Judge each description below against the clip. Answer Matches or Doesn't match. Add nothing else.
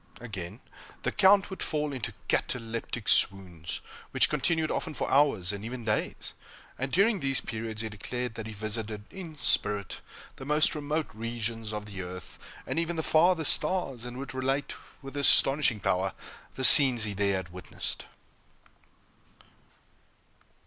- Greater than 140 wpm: Matches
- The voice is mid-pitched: Doesn't match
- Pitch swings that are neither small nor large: Doesn't match